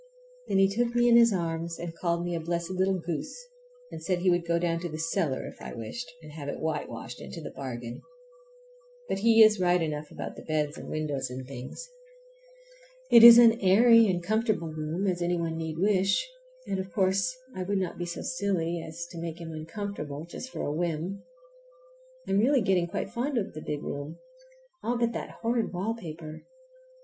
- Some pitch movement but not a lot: Yes, average, 4.1 semitones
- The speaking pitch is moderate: Yes, medium, 175 Hz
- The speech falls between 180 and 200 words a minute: Yes, average, 195 wpm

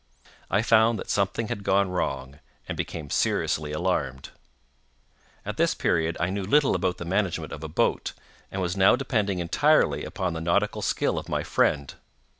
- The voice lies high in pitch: No, very low, 90 Hz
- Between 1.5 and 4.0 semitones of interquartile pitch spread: Yes, average, 3.7 semitones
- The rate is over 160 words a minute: Yes, average, 170 wpm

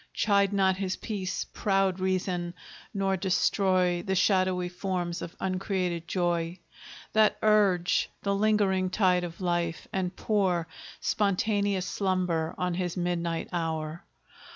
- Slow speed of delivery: Yes, slow, 120 wpm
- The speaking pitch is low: No, medium, 185 Hz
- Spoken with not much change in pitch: Yes, narrow, 2.0 semitones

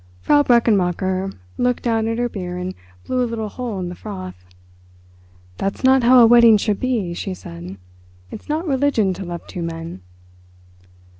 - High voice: Yes, high, 210 Hz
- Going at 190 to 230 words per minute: No, average, 165 wpm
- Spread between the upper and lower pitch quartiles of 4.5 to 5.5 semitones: Yes, average, 5.2 semitones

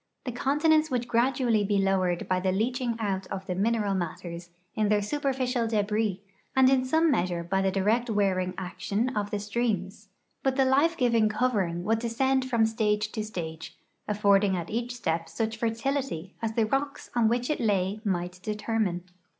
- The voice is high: Yes, high, 215 Hz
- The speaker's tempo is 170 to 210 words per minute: Yes, average, 175 wpm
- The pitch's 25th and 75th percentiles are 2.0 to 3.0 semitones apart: No, average, 4.2 semitones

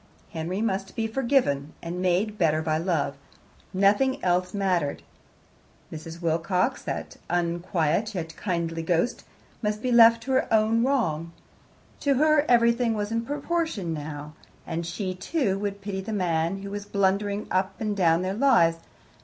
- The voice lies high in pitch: Yes, high, 195 Hz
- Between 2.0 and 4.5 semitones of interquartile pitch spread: No, average, 5.0 semitones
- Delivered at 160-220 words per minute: No, average, 150 wpm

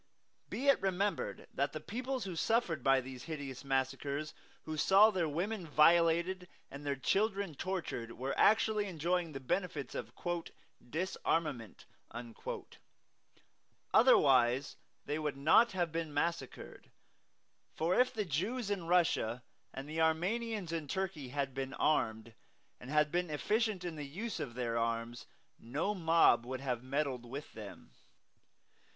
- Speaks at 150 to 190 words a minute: No, average, 140 wpm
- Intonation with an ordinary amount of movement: No, wide, 5.7 semitones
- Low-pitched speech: No, medium, 155 Hz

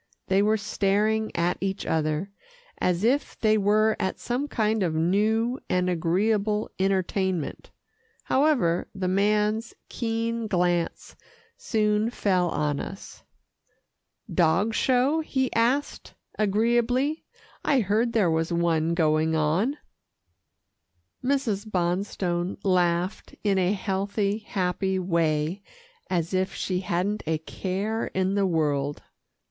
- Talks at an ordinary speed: No, slow, 115 wpm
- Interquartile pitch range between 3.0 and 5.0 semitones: Yes, average, 3.9 semitones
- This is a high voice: Yes, high, 195 Hz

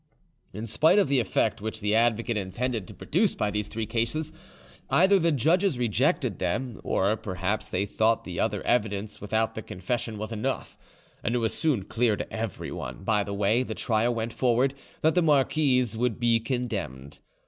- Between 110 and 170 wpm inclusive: No, average, 180 wpm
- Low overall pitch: Yes, low, 115 Hz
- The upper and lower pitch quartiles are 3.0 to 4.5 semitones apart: Yes, average, 3.4 semitones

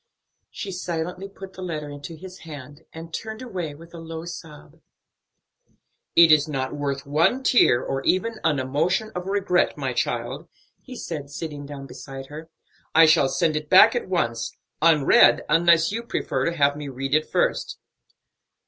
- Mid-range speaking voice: Yes, medium, 160 Hz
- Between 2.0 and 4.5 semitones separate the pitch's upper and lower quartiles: Yes, average, 4.1 semitones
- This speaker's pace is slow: No, average, 165 wpm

